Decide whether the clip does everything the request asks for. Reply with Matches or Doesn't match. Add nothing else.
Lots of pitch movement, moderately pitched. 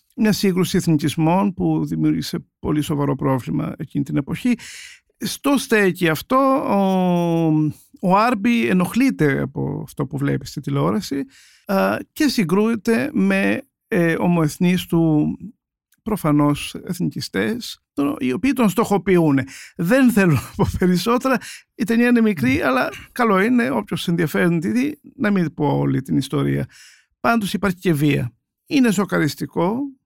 Matches